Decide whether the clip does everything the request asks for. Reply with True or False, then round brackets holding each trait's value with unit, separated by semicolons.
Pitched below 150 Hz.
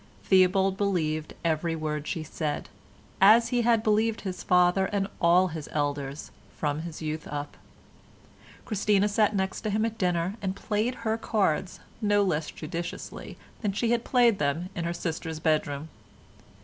False (185 Hz)